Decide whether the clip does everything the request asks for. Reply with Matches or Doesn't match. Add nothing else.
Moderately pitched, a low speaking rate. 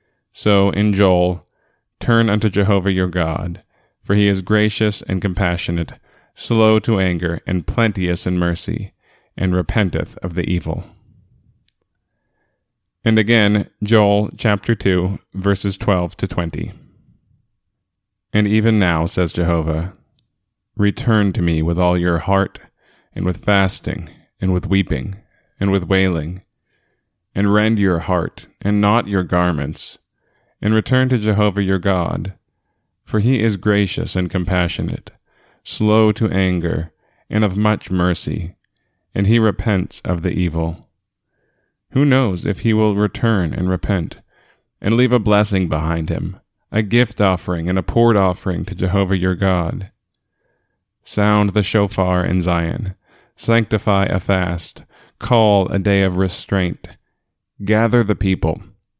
Doesn't match